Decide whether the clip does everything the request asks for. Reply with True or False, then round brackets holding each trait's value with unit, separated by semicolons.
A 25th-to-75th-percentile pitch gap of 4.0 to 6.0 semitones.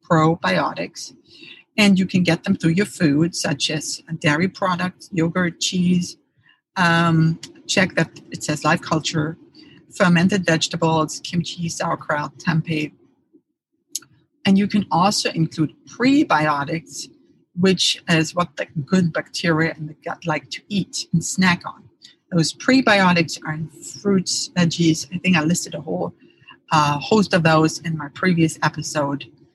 False (3.1 semitones)